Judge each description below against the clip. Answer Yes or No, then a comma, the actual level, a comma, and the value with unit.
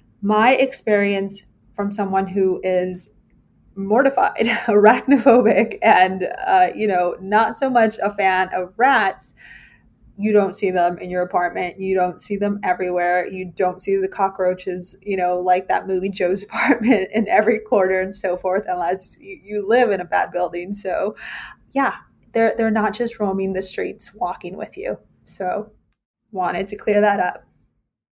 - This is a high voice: Yes, high, 195 Hz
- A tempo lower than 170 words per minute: Yes, average, 160 wpm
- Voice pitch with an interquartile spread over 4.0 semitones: No, average, 3.0 semitones